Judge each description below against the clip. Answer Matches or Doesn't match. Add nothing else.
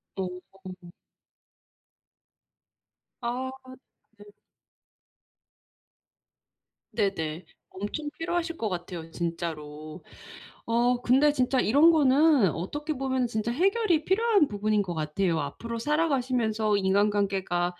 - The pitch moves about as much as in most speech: Doesn't match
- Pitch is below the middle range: Doesn't match